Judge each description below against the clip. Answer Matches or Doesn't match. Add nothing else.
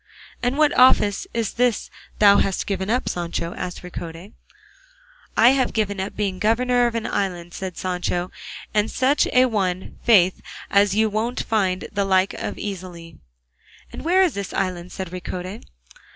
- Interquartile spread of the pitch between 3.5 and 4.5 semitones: Matches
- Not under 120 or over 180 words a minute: Matches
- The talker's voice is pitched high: Matches